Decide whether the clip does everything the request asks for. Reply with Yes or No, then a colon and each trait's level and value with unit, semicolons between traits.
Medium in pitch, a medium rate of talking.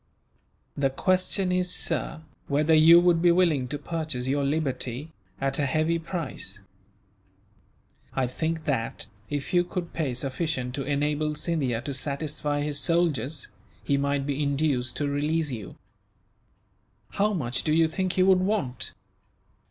Yes: medium, 150 Hz; average, 145 wpm